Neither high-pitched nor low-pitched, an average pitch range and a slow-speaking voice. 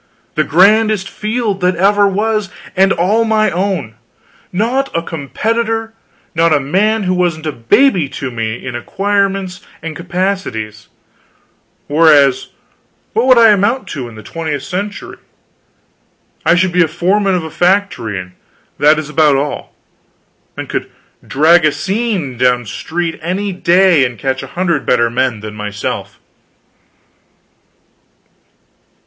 No: medium, 175 Hz; wide, 6.2 semitones; slow, 130 wpm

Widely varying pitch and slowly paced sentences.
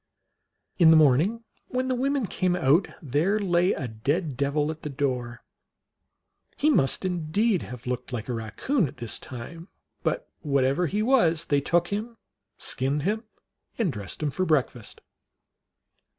No: wide, 6.8 semitones; average, 150 wpm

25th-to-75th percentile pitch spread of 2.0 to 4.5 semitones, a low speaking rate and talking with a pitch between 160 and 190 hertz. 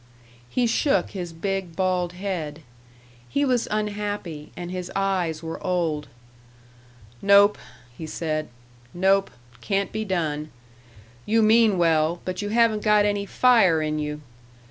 Yes: average, 4.2 semitones; slow, 130 wpm; medium, 185 Hz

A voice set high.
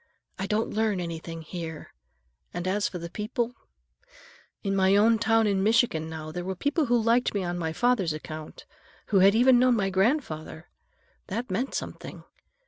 Yes: high, 200 Hz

